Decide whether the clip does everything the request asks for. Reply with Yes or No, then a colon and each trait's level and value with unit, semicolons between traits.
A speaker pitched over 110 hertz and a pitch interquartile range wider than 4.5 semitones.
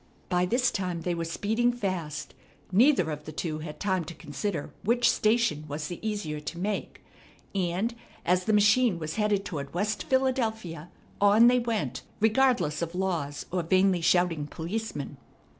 Yes: medium, 185 Hz; average, 5.2 semitones